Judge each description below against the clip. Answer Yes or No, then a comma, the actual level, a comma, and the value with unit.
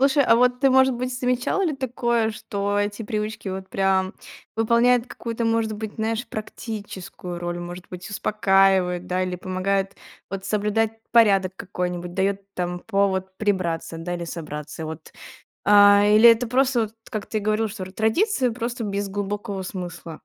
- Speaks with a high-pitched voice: Yes, high, 205 Hz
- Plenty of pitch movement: No, average, 3.4 semitones